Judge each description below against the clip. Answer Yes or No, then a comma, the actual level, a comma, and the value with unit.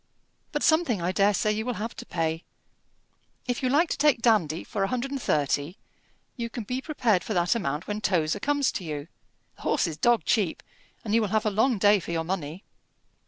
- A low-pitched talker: No, high, 210 Hz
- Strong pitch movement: Yes, wide, 6.0 semitones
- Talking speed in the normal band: No, fast, 215 wpm